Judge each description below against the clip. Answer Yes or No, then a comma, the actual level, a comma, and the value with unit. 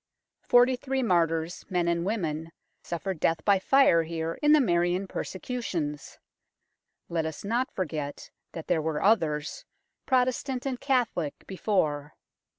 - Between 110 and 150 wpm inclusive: Yes, slow, 135 wpm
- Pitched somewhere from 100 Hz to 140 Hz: No, medium, 175 Hz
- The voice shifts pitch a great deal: Yes, wide, 7.1 semitones